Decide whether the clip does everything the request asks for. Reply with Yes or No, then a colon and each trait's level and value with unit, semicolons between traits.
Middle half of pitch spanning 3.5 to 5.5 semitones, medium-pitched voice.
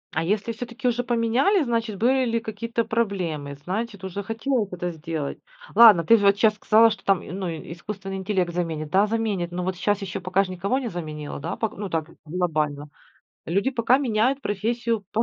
No: average, 4.7 semitones; high, 200 Hz